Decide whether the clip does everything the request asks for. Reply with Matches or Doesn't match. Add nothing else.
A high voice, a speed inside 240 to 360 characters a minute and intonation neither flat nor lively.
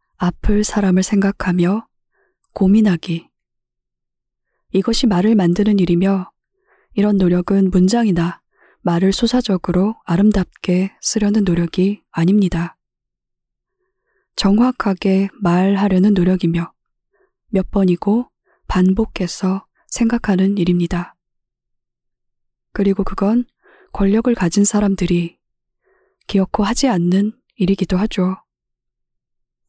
Doesn't match